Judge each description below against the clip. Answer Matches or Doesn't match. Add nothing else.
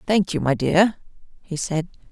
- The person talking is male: Doesn't match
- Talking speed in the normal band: Matches